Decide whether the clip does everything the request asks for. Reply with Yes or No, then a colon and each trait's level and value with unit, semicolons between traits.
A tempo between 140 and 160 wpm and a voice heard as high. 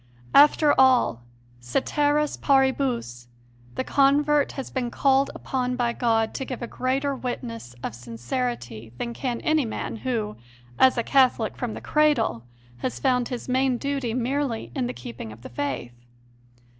Yes: average, 150 wpm; high, 245 Hz